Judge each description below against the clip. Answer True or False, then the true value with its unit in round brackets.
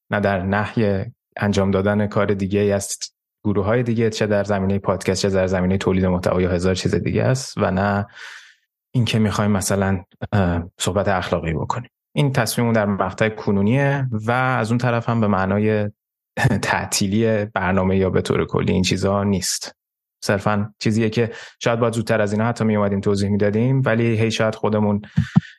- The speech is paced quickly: True (165 wpm)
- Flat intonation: True (2.2 semitones)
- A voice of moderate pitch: False (105 Hz)